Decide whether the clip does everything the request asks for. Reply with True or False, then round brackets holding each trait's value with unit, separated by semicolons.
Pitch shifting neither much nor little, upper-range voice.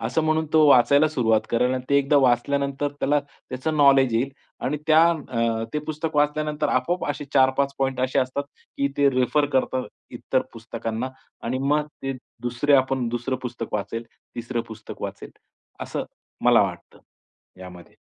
False (3.3 semitones; 135 Hz)